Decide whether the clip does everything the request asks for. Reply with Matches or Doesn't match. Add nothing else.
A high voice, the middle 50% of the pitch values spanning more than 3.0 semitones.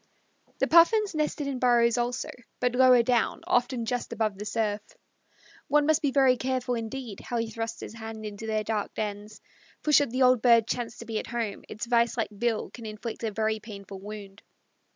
Doesn't match